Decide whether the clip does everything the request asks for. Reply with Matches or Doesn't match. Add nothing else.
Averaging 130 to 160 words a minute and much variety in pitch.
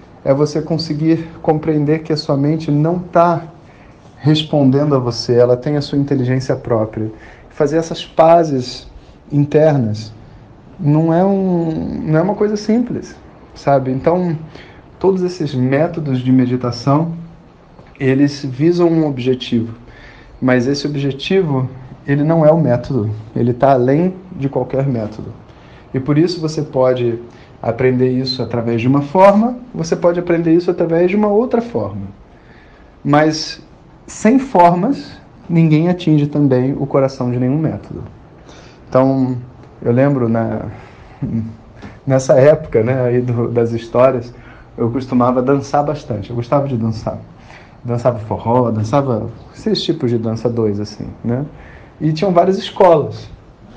Doesn't match